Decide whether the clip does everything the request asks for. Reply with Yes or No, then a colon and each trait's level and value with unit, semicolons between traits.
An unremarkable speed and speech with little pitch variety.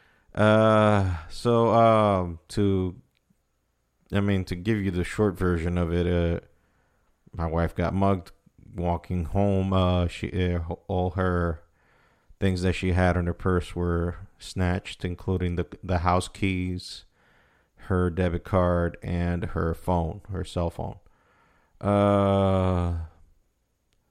No: slow, 125 wpm; narrow, 2.1 semitones